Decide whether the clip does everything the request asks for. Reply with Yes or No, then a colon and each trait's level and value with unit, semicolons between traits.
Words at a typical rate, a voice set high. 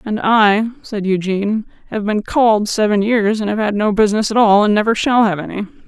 No: fast, 215 wpm; high, 210 Hz